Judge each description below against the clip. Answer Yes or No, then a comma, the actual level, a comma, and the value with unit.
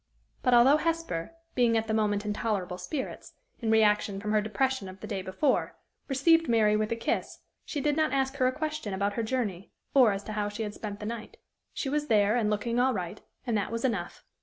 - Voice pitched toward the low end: No, high, 220 Hz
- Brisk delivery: Yes, fast, 225 wpm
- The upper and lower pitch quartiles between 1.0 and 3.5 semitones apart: No, average, 4.1 semitones